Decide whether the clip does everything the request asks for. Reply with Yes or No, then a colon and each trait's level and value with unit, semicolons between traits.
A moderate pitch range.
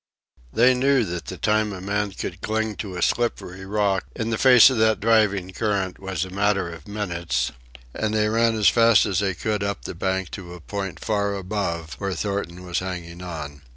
Yes: average, 3.0 semitones